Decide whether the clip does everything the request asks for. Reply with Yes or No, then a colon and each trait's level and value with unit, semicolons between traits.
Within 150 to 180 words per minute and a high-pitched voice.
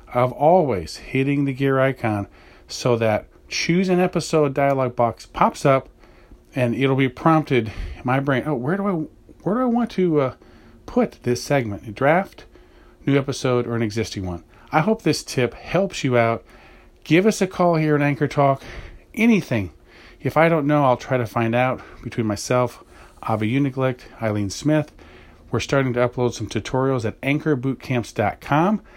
No: average, 170 wpm; low, 130 Hz